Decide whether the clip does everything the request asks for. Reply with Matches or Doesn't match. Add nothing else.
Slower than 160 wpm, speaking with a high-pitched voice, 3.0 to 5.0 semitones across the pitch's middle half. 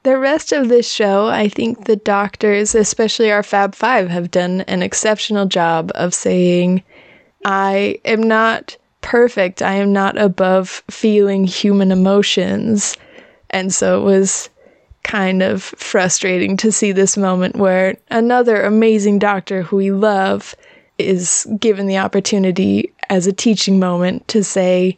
Doesn't match